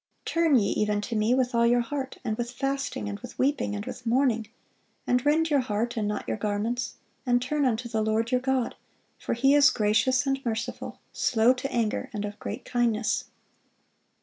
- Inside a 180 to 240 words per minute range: Yes, average, 195 wpm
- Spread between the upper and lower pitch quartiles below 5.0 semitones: Yes, average, 3.3 semitones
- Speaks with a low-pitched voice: No, high, 240 Hz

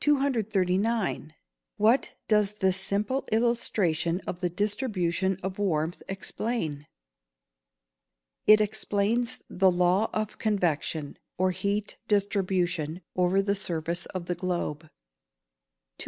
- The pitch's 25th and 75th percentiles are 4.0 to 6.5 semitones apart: No, average, 3.2 semitones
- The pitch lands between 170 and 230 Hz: Yes, high, 190 Hz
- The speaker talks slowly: Yes, slow, 100 wpm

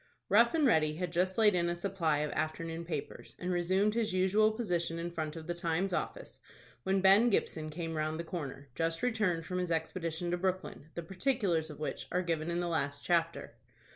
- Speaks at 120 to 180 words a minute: No, average, 200 wpm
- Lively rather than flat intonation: No, average, 2.7 semitones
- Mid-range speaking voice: Yes, medium, 175 Hz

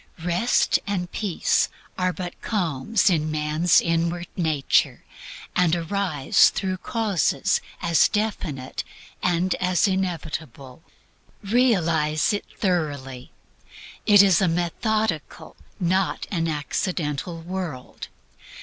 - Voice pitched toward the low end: No, medium, 175 Hz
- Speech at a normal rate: No, slow, 95 wpm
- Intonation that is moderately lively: Yes, average, 3.5 semitones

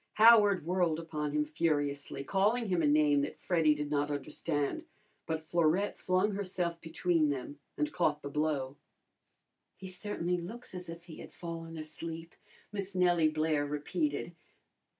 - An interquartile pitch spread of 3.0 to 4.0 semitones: Yes, average, 3.4 semitones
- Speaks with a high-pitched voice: No, medium, 165 Hz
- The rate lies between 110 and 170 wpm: Yes, average, 150 wpm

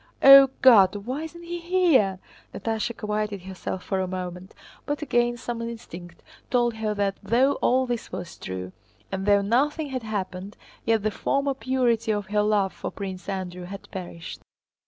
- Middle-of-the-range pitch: No, high, 215 Hz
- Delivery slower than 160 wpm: No, average, 165 wpm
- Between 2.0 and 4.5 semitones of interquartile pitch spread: No, average, 5.0 semitones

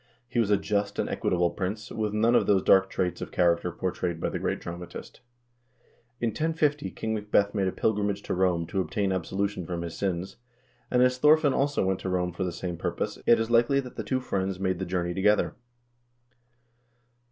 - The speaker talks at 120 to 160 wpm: No, average, 200 wpm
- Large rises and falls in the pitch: No, average, 3.8 semitones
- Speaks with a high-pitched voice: No, very low, 95 Hz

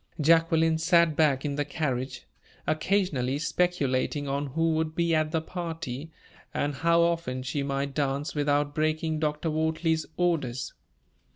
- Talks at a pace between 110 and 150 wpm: Yes, slow, 135 wpm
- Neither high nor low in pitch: Yes, medium, 155 Hz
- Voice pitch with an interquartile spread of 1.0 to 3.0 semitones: Yes, average, 2.7 semitones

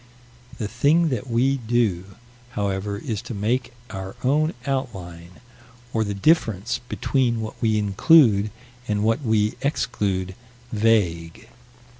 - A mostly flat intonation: No, average, 3.9 semitones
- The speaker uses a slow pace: Yes, slow, 120 wpm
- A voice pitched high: No, low, 110 Hz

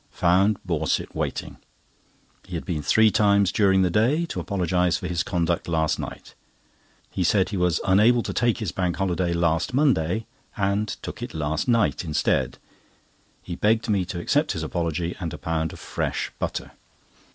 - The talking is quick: No, average, 170 wpm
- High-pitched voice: No, very low, 90 Hz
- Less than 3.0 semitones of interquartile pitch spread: No, average, 3.7 semitones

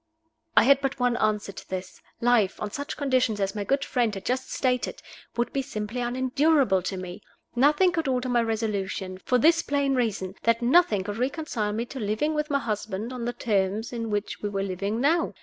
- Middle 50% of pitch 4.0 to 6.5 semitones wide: Yes, average, 4.6 semitones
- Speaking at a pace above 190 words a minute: Yes, average, 200 wpm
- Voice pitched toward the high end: Yes, high, 235 Hz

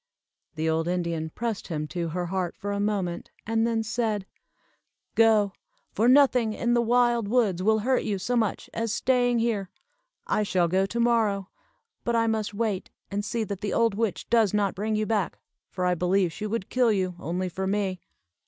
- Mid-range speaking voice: No, high, 210 Hz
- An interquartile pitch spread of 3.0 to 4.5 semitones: Yes, average, 3.6 semitones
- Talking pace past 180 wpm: Yes, average, 190 wpm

